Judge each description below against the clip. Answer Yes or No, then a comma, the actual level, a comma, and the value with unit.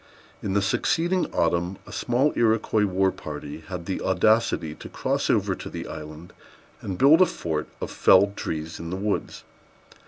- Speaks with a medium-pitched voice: No, very low, 95 Hz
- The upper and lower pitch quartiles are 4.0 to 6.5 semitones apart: Yes, average, 4.7 semitones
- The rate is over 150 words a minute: Yes, average, 165 wpm